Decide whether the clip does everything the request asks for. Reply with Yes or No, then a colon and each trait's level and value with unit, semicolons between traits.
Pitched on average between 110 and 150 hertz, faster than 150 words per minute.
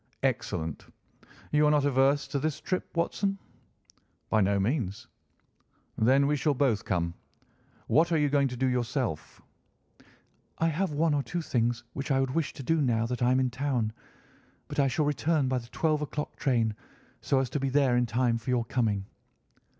Yes: low, 135 Hz; average, 185 wpm